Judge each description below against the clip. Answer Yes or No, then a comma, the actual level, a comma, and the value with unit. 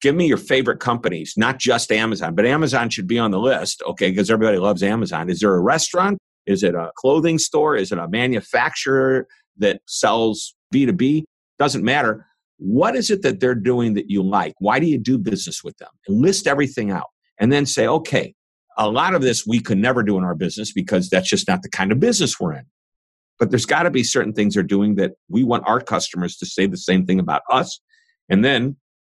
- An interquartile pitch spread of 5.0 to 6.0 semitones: Yes, wide, 5.5 semitones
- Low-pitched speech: Yes, low, 110 Hz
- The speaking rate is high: Yes, fast, 215 wpm